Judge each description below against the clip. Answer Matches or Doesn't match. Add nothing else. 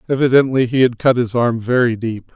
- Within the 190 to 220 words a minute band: Matches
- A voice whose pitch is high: Doesn't match